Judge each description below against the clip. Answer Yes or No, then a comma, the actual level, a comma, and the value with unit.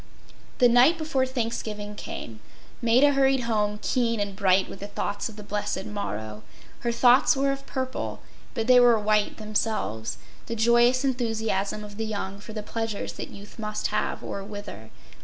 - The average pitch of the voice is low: No, high, 220 Hz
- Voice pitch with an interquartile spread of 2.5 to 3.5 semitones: Yes, average, 3.2 semitones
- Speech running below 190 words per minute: Yes, average, 165 wpm